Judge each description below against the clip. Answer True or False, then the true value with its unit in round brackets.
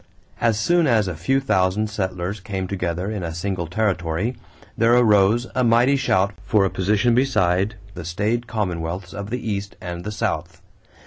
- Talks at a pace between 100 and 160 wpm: False (170 wpm)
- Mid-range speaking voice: False (100 Hz)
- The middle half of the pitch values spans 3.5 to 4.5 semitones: True (4.0 semitones)